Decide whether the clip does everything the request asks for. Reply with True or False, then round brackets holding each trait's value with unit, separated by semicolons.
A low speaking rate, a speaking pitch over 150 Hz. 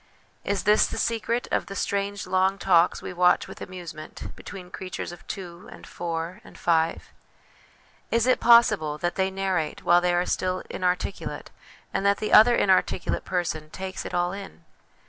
False (165 wpm; 185 Hz)